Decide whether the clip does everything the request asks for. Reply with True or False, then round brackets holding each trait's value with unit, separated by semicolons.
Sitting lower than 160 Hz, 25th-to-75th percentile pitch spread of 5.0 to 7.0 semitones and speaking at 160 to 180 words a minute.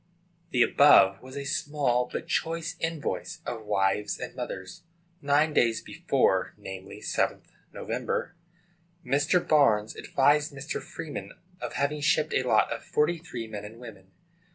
False (140 Hz; 5.4 semitones; 145 wpm)